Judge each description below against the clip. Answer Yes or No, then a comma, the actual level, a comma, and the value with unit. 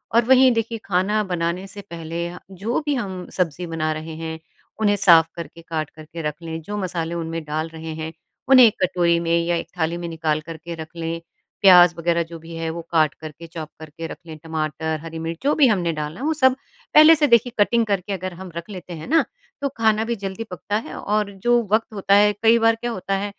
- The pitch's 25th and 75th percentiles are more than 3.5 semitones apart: Yes, average, 4.2 semitones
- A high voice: No, medium, 175 Hz